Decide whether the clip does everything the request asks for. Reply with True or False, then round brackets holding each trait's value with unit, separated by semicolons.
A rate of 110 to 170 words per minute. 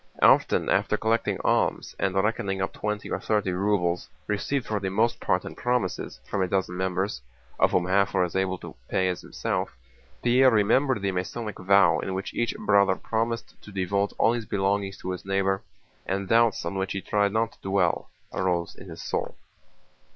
False (190 wpm)